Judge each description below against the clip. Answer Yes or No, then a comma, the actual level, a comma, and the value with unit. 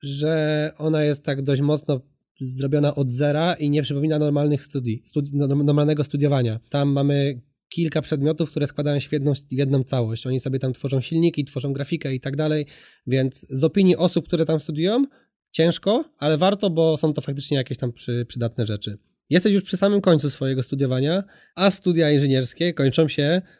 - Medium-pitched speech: Yes, medium, 145 Hz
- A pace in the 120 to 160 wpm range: No, fast, 180 wpm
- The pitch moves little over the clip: No, average, 3.0 semitones